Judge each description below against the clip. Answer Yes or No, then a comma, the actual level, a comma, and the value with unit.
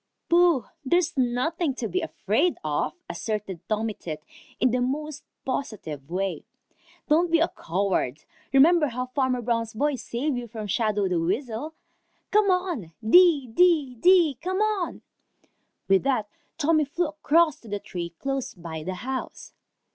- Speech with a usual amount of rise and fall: No, wide, 7.3 semitones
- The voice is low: No, very high, 255 Hz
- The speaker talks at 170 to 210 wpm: No, average, 145 wpm